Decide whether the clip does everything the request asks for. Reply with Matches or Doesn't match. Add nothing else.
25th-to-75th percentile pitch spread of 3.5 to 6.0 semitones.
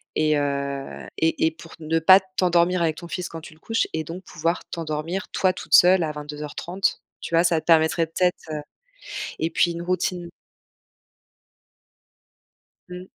Doesn't match